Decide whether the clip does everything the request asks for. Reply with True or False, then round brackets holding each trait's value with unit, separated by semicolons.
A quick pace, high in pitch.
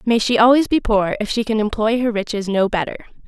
True (240 wpm; 220 Hz)